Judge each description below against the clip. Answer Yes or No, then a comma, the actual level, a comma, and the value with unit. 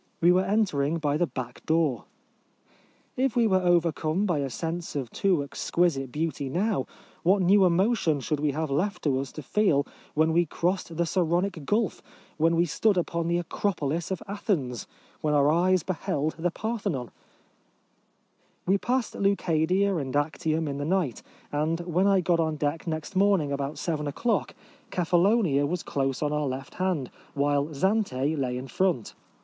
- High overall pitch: No, medium, 165 Hz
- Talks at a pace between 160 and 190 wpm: Yes, average, 165 wpm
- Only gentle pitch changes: No, average, 4.4 semitones